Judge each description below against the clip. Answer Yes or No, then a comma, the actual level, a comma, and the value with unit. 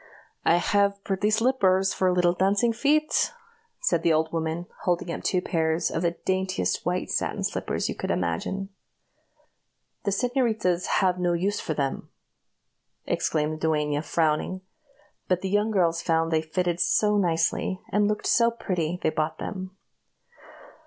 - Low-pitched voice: No, medium, 180 Hz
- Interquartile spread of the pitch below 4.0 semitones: Yes, average, 3.6 semitones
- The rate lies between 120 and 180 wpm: Yes, average, 150 wpm